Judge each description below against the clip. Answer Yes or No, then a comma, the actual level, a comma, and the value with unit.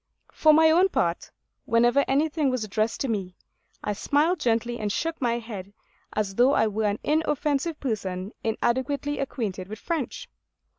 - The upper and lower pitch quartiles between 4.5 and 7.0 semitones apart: Yes, wide, 5.5 semitones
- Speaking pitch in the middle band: No, high, 240 Hz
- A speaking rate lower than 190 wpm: Yes, average, 155 wpm